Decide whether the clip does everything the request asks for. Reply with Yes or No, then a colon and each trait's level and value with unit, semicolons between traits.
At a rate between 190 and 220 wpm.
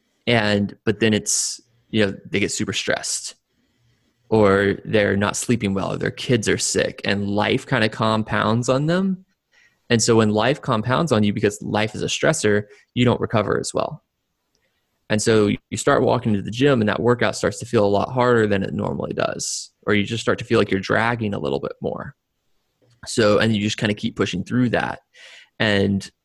Yes: fast, 205 wpm